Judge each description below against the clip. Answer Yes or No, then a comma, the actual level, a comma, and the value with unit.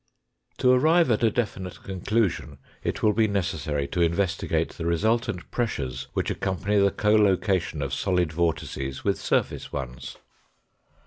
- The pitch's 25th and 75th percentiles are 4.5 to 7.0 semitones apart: Yes, average, 5.1 semitones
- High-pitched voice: No, very low, 95 Hz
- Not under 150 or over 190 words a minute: No, slow, 135 wpm